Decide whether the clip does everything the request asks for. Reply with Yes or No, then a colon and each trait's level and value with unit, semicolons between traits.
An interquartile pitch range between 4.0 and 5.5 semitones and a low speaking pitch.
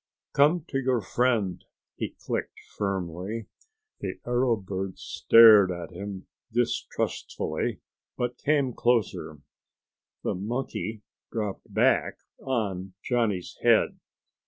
Yes: average, 4.4 semitones; low, 110 Hz